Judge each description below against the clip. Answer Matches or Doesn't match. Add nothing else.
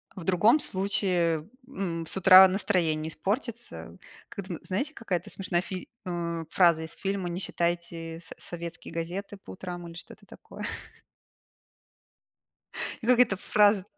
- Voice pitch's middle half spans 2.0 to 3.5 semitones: Matches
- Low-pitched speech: Doesn't match